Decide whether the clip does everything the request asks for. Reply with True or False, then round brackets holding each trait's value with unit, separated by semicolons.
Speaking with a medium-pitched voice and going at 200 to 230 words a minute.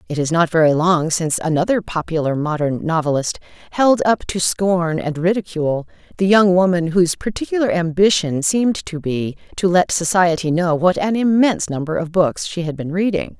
False (170 Hz; 175 wpm)